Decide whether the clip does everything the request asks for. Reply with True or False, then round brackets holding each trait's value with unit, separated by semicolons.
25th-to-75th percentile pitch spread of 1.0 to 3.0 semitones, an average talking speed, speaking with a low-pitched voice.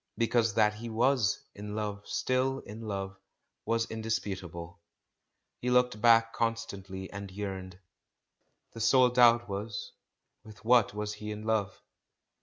False (2.6 semitones; 130 wpm; 110 Hz)